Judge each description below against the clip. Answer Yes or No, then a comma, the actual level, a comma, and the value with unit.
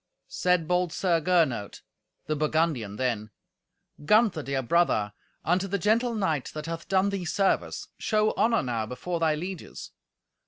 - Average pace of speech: Yes, average, 145 wpm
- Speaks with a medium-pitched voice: Yes, medium, 165 Hz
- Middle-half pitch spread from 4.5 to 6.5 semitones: Yes, average, 5.3 semitones